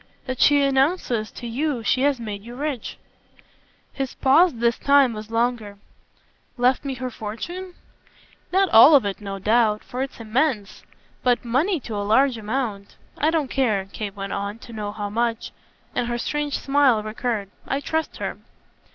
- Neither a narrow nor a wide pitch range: Yes, average, 4.3 semitones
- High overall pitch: Yes, high, 240 Hz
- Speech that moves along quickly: No, average, 170 wpm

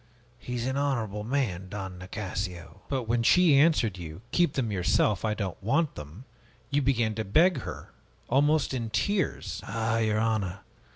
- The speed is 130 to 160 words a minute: No, average, 170 wpm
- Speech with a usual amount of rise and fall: No, wide, 5.7 semitones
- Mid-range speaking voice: No, low, 110 Hz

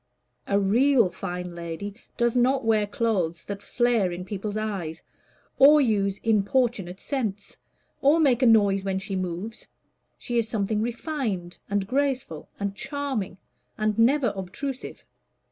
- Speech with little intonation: No, average, 4.2 semitones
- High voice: Yes, high, 215 Hz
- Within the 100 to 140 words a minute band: Yes, slow, 135 wpm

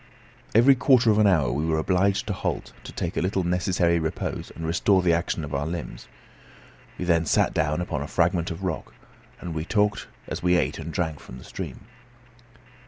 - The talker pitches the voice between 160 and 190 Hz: No, very low, 85 Hz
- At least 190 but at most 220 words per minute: Yes, average, 200 wpm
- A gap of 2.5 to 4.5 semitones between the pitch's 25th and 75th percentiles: Yes, average, 3.1 semitones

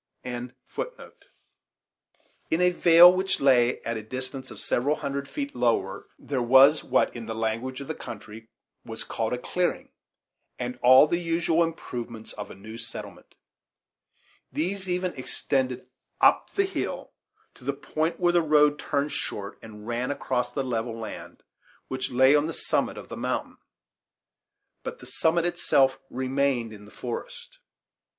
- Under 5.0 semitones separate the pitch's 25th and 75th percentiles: No, average, 5.3 semitones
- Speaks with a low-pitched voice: Yes, low, 130 Hz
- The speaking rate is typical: Yes, average, 150 wpm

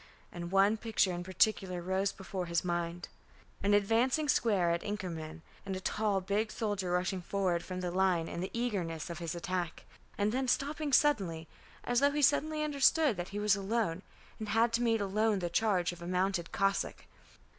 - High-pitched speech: Yes, high, 195 Hz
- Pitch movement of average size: Yes, average, 4.1 semitones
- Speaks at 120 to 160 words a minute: No, average, 185 wpm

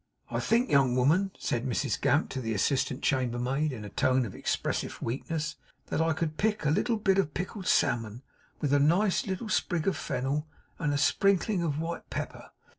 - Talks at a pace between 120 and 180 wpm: No, average, 190 wpm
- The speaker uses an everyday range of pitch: No, wide, 5.9 semitones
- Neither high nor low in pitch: Yes, medium, 150 Hz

